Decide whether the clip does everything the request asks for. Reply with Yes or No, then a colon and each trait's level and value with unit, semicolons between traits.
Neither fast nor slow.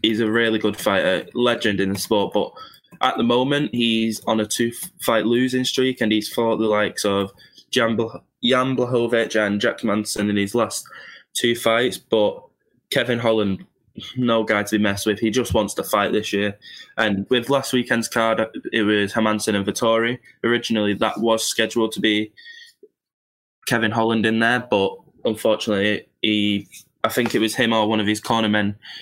Yes: average, 175 wpm